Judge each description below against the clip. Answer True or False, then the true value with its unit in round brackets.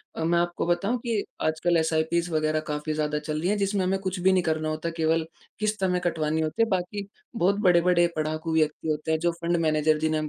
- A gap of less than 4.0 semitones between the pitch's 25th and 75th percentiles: True (2.6 semitones)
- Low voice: False (165 Hz)